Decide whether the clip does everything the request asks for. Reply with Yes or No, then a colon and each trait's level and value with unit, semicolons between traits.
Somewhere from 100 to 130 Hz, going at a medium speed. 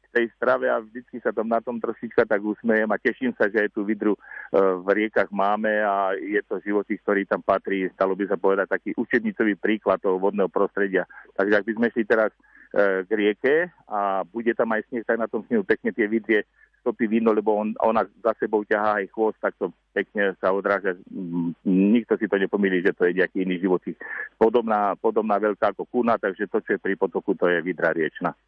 No: low, 105 Hz; fast, 210 wpm